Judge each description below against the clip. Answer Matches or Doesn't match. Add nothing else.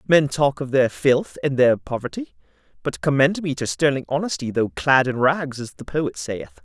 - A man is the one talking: Matches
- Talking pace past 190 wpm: Matches